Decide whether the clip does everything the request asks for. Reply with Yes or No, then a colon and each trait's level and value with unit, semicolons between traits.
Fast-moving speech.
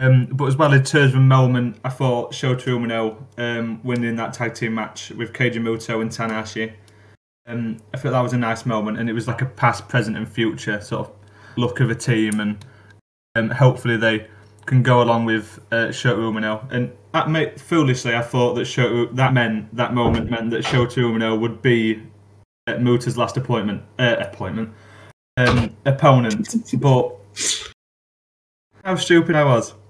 No: average, 180 wpm